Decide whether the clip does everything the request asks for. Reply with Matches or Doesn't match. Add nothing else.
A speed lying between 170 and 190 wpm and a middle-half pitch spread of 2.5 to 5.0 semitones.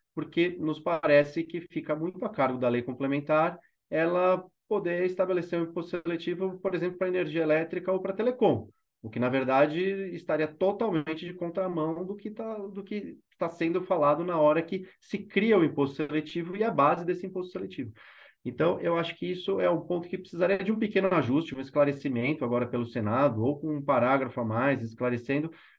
Matches